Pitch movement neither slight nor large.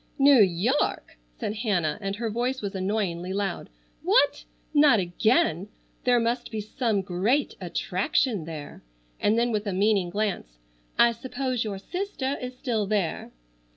Yes: average, 4.5 semitones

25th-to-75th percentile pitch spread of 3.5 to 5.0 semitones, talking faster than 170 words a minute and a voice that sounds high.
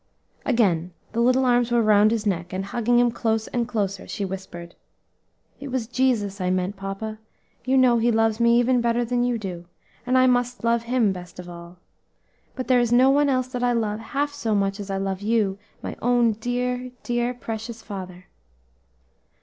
Yes: average, 3.8 semitones; average, 190 wpm; high, 230 Hz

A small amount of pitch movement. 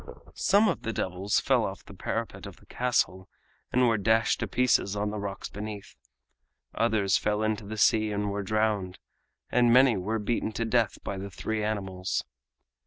Yes: narrow, 2.0 semitones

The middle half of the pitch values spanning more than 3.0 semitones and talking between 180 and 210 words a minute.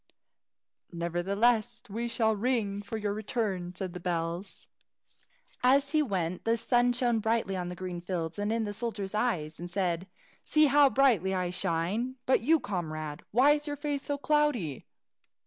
No: wide, 5.5 semitones; average, 160 wpm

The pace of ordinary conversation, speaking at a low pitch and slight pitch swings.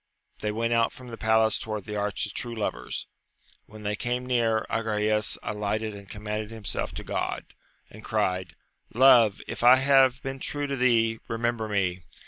Yes: average, 170 wpm; low, 110 Hz; narrow, 2.3 semitones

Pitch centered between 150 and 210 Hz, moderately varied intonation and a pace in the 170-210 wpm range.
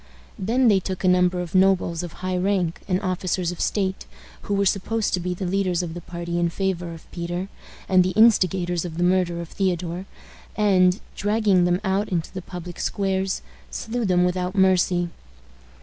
No: medium, 185 Hz; narrow, 1.6 semitones; average, 180 wpm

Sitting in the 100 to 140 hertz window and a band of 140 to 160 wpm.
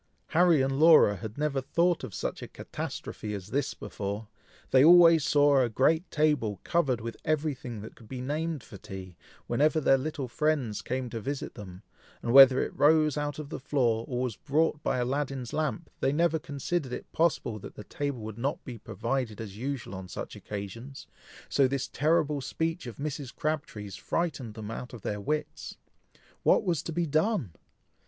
No: low, 135 Hz; average, 185 wpm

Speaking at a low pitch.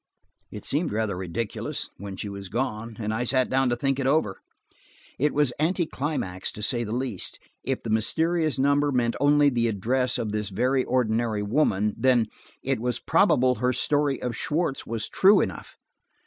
Yes: low, 125 Hz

